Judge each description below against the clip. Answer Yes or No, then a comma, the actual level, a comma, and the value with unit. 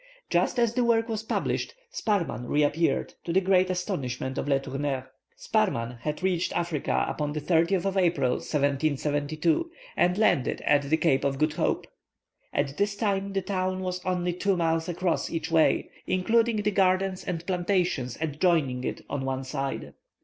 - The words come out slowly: No, average, 165 wpm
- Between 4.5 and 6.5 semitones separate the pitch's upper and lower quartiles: Yes, average, 4.9 semitones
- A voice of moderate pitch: Yes, medium, 170 Hz